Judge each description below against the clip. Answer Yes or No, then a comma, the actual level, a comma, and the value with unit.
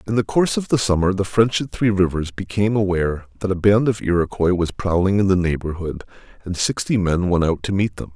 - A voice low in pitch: Yes, very low, 95 Hz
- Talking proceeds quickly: Yes, fast, 230 wpm